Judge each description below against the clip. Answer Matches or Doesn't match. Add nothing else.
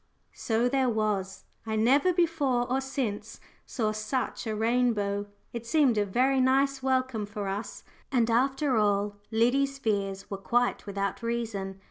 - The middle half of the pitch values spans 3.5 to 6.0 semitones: Matches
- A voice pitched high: Matches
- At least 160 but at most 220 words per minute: Doesn't match